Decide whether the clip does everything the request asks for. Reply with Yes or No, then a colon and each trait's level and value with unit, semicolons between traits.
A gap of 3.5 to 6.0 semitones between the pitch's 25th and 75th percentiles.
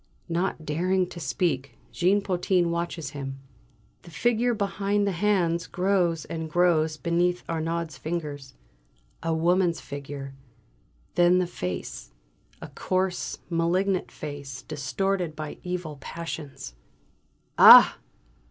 No: average, 3.0 semitones